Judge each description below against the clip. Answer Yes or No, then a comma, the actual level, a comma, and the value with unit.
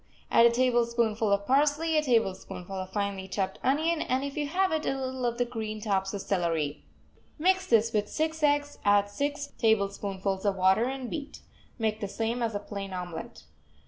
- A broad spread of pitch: Yes, wide, 5.8 semitones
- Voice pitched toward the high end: Yes, high, 225 Hz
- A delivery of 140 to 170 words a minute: No, average, 185 wpm